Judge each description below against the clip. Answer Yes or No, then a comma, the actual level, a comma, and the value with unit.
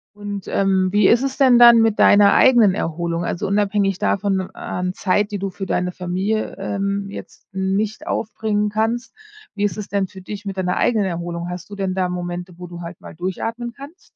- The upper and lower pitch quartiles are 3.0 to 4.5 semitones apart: No, narrow, 2.5 semitones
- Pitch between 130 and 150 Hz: No, high, 195 Hz